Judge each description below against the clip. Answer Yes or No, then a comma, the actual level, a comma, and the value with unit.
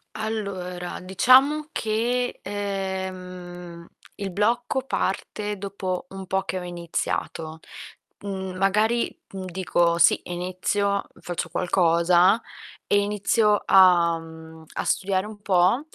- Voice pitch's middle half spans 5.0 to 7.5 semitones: No, narrow, 2.6 semitones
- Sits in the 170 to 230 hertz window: Yes, high, 190 Hz